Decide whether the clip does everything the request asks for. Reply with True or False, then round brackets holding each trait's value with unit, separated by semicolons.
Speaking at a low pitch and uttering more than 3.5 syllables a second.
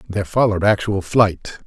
True (100 Hz; 5.6 syllables/s)